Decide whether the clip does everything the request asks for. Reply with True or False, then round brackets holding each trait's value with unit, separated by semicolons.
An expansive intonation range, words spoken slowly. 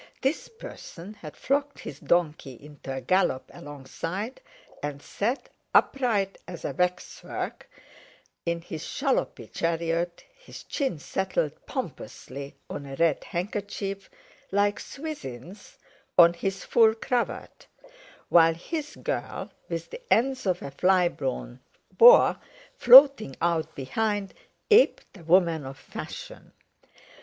True (6.2 semitones; 115 wpm)